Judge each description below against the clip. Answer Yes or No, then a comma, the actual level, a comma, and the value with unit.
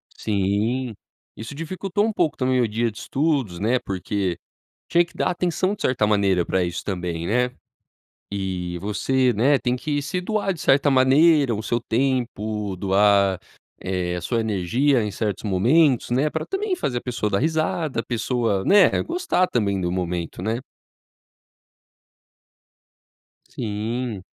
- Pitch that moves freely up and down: Yes, wide, 6.3 semitones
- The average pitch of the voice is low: Yes, low, 115 Hz